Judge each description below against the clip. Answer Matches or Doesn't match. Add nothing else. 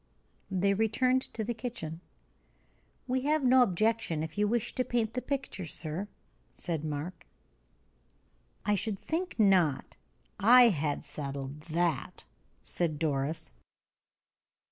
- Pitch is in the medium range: Doesn't match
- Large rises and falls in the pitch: Matches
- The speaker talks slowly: Matches